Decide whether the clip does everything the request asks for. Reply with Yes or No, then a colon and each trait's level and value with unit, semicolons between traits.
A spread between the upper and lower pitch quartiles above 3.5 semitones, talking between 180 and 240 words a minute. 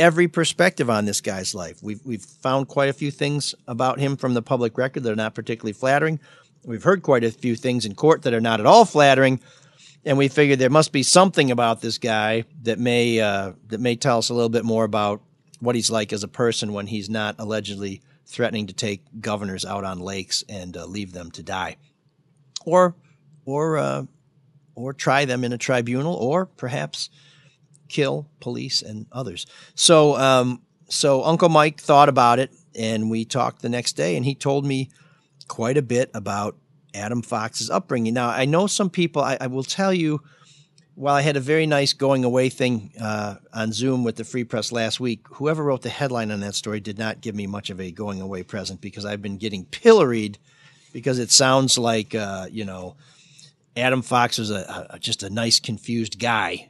Yes: average, 4.8 semitones; average, 200 wpm